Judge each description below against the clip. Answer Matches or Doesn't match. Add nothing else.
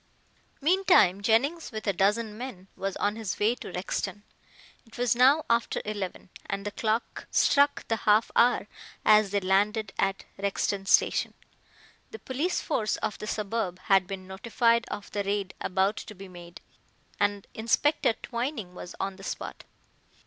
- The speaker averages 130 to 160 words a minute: Matches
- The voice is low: Doesn't match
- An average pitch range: Matches